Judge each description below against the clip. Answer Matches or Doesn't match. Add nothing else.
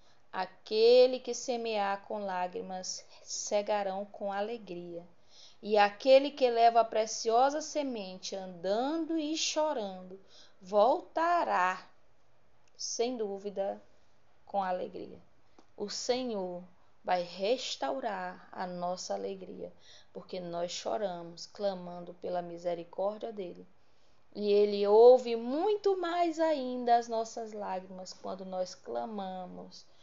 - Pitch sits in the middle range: Doesn't match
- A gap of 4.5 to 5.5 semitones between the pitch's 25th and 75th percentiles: Matches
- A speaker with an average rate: Doesn't match